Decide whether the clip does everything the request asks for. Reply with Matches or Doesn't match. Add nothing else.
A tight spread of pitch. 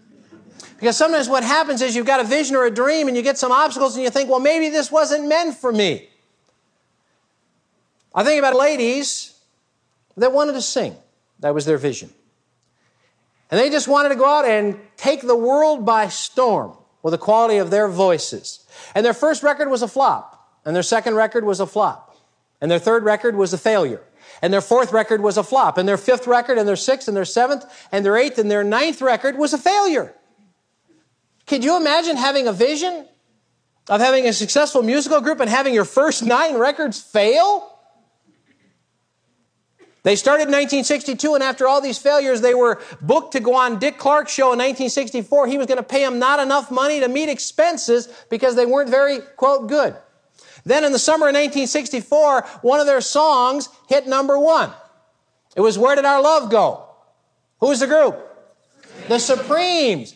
Doesn't match